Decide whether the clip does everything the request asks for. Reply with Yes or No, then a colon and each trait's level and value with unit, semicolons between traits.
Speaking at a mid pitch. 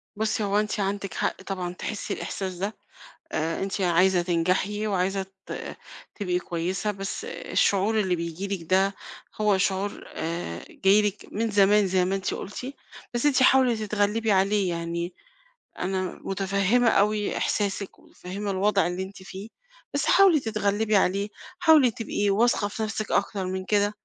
No: high, 200 Hz